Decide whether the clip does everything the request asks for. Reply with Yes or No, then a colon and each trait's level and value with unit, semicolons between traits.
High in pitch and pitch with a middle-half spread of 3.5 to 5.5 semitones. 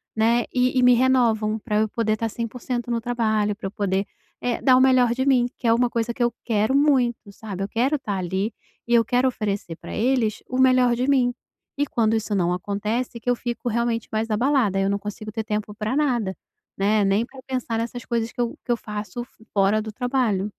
No: high, 230 Hz; average, 2.7 semitones